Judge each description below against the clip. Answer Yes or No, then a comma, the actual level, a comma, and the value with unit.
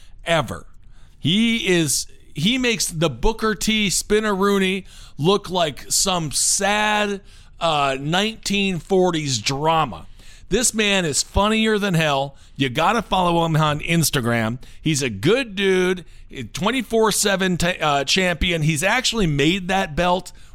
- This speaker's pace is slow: Yes, slow, 125 wpm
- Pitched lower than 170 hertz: No, medium, 175 Hz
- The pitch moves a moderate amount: No, wide, 6.2 semitones